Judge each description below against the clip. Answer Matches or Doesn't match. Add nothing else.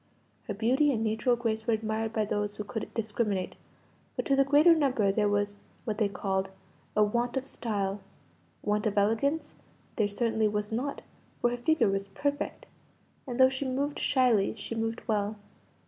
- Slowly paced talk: Doesn't match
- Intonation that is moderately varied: Matches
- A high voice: Matches